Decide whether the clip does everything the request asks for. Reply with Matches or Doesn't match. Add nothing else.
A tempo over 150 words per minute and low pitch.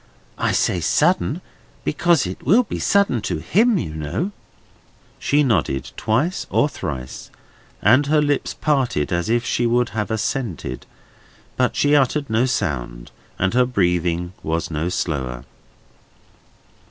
Doesn't match